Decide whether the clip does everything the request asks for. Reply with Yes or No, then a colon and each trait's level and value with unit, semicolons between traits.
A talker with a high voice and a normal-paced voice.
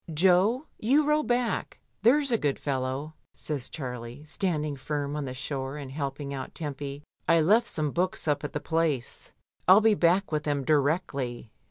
No: medium, 150 Hz; average, 170 wpm